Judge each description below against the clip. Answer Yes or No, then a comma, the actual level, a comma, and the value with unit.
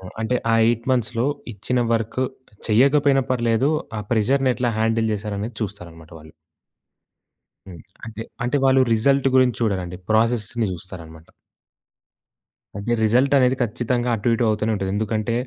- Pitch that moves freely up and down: No, average, 3.3 semitones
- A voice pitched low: Yes, low, 115 Hz